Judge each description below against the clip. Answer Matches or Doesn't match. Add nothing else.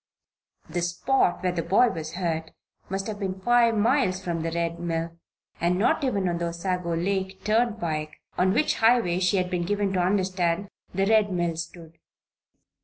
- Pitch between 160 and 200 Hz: Matches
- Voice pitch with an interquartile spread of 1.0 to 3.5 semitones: Matches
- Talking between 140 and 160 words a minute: Doesn't match